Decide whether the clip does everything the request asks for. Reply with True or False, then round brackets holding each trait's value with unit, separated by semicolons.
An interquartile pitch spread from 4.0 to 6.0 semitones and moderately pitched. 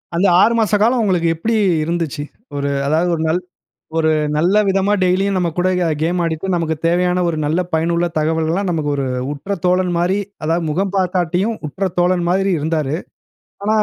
False (2.9 semitones; 175 Hz)